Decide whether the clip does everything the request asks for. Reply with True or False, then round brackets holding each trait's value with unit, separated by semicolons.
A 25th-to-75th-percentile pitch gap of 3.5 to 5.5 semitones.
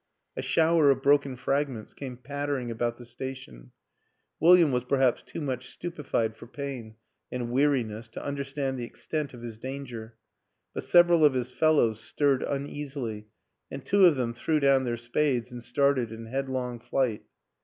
False (3.1 semitones)